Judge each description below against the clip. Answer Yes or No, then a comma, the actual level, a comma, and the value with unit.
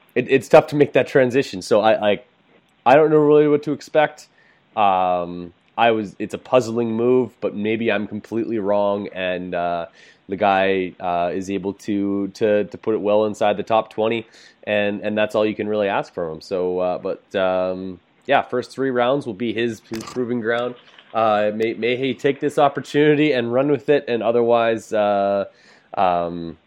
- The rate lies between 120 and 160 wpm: No, average, 190 wpm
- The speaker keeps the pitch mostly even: No, average, 3.9 semitones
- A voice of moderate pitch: No, low, 110 Hz